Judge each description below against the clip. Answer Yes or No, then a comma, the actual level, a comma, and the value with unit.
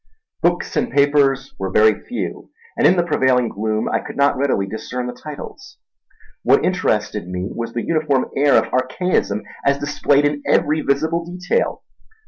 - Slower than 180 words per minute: Yes, average, 160 wpm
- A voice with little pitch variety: No, average, 4.9 semitones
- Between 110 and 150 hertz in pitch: Yes, medium, 140 Hz